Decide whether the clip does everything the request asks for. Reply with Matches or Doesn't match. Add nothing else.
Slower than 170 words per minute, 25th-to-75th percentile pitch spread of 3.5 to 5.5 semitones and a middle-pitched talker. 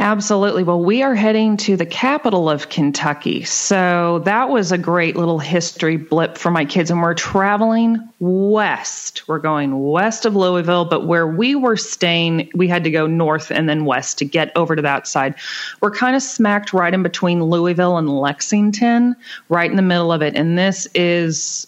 Doesn't match